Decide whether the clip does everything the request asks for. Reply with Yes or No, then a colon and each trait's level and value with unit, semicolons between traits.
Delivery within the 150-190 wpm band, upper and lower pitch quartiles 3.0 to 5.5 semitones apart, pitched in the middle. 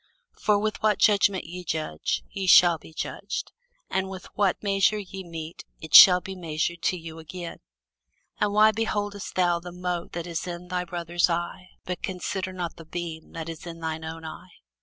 No: average, 185 wpm; narrow, 2.4 semitones; medium, 175 Hz